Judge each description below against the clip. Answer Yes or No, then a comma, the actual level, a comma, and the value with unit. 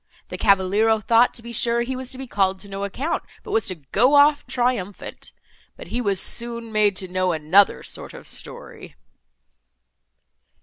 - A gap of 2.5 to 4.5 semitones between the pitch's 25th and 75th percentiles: Yes, average, 3.9 semitones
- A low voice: No, high, 220 Hz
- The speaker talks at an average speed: Yes, average, 175 wpm